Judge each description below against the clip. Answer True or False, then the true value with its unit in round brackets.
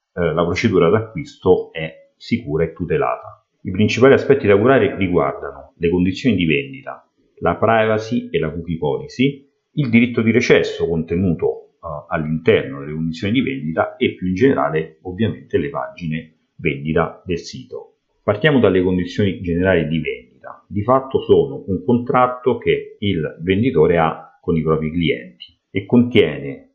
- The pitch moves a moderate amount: False (8.1 semitones)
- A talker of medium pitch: False (110 Hz)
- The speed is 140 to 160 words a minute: True (145 wpm)